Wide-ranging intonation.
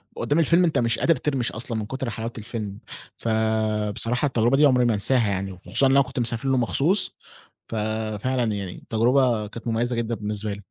No: average, 3.3 semitones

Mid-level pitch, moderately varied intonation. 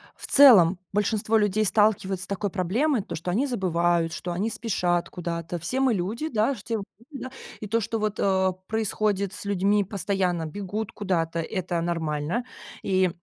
No: high, 195 Hz; average, 3.6 semitones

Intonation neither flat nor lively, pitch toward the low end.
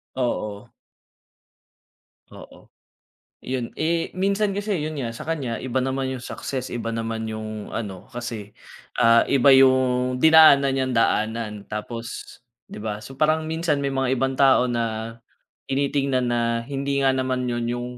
Yes: average, 3.2 semitones; low, 130 Hz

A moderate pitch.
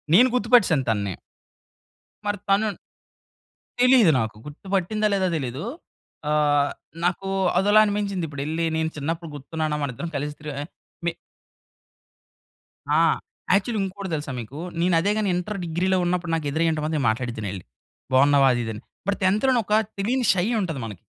Yes: medium, 165 Hz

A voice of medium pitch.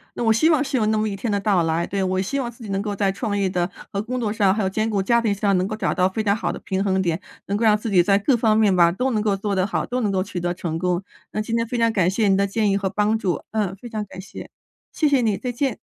No: high, 205 Hz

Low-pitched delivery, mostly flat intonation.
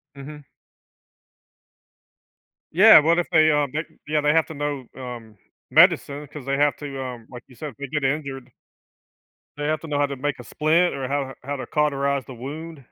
No: medium, 145 Hz; narrow, 2.2 semitones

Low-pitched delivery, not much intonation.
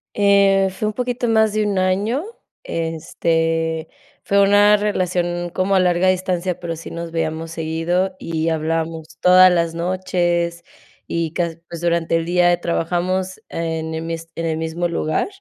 No: medium, 175 Hz; narrow, 2.3 semitones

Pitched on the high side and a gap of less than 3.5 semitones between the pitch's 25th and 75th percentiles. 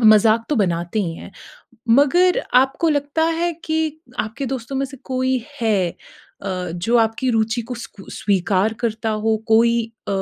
No: high, 230 Hz; average, 4.1 semitones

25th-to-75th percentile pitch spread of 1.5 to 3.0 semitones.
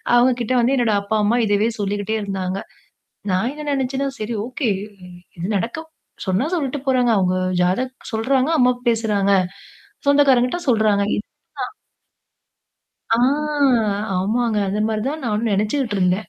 No: average, 4.0 semitones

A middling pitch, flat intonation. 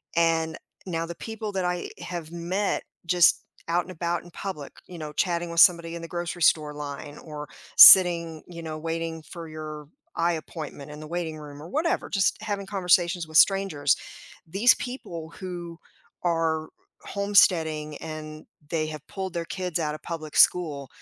Yes: medium, 165 Hz; narrow, 2.3 semitones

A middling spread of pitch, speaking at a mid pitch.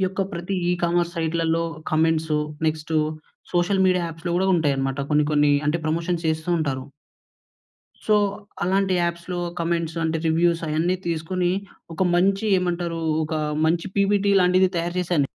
No: narrow, 2.1 semitones; medium, 170 Hz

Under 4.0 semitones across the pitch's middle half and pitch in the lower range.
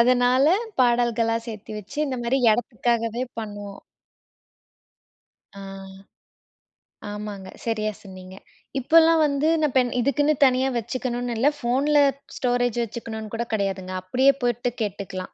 No: average, 3.1 semitones; high, 235 Hz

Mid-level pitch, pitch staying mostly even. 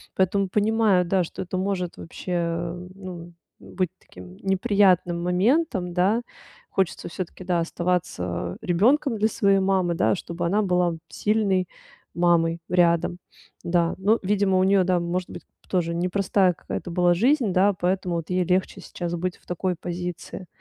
Yes: medium, 180 Hz; narrow, 2.0 semitones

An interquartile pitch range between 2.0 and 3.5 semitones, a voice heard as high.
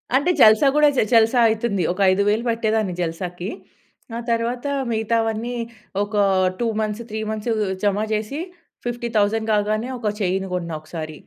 Yes: narrow, 2.4 semitones; high, 215 Hz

